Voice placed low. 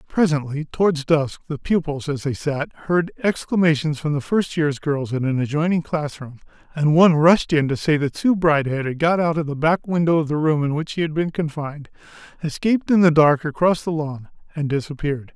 No: medium, 155 Hz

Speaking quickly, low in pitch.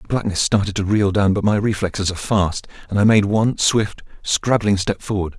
Yes: fast, 210 wpm; low, 100 Hz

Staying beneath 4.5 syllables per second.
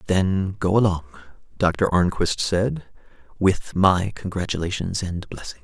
Yes: 4.2 syllables/s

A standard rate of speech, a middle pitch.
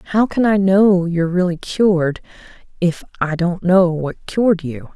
Yes: average, 155 wpm; medium, 180 Hz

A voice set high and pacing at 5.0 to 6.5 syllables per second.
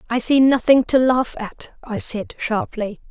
No: high, 240 Hz; 4.1 syllables/s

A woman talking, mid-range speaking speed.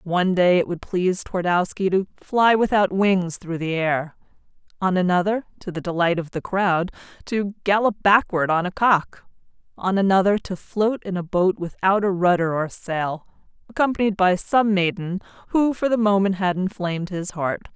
Yes: female; average, 170 wpm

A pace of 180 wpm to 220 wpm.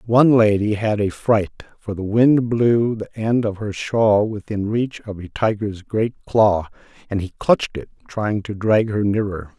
Yes: average, 190 wpm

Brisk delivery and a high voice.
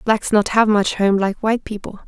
Yes: fast, 230 wpm; high, 210 Hz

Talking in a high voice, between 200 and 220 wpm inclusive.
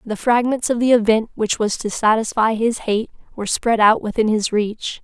Yes: high, 220 Hz; fast, 205 wpm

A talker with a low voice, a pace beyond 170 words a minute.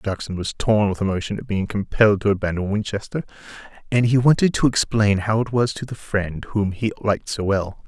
Yes: low, 105 Hz; fast, 205 wpm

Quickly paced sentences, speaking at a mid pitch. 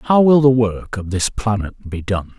No: fast, 225 wpm; low, 110 Hz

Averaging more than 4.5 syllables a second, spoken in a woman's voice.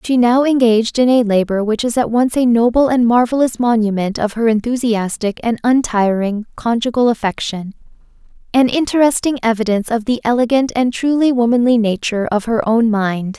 Yes: 5.4 syllables/s; female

